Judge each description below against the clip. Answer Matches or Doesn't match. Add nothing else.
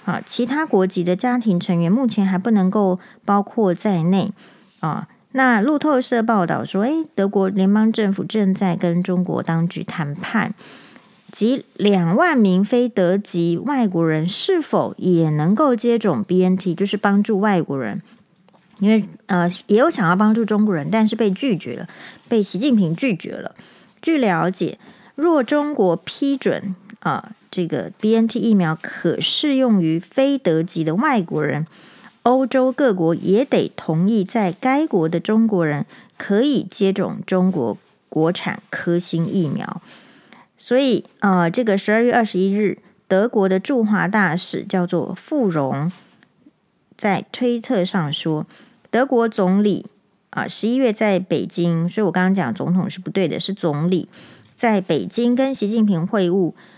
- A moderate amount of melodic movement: Matches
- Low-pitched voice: Doesn't match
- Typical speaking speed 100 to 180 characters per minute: Doesn't match